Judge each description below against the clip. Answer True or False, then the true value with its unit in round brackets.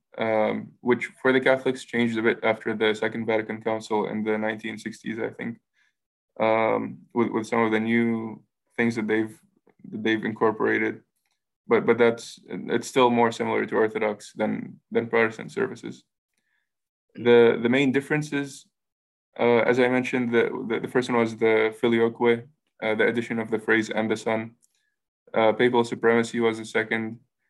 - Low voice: True (115 Hz)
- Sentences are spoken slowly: False (160 wpm)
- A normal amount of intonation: False (1.6 semitones)